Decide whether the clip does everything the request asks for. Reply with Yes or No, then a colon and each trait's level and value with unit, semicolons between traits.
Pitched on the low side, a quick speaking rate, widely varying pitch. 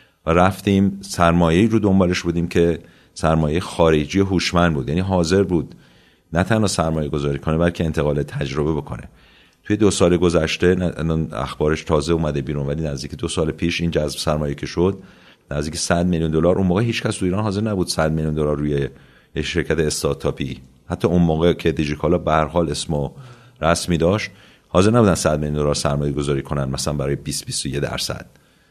No: very low, 85 Hz; fast, 175 wpm; average, 3.1 semitones